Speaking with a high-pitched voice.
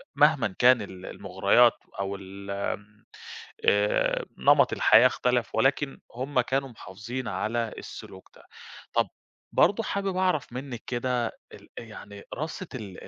No: low, 120 Hz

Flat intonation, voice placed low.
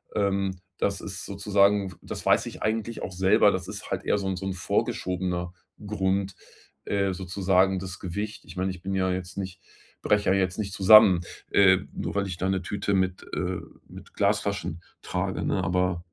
Yes: narrow, 1.4 semitones; very low, 95 Hz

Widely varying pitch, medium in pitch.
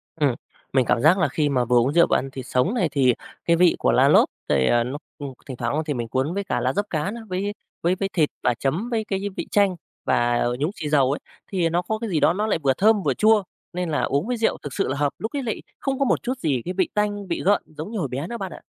Yes: wide, 7.0 semitones; medium, 165 Hz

